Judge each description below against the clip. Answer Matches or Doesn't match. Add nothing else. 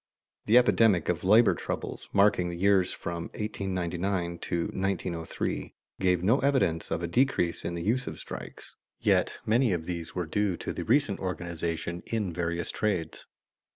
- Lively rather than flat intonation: Doesn't match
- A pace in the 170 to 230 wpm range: Doesn't match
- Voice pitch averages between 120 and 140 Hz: Doesn't match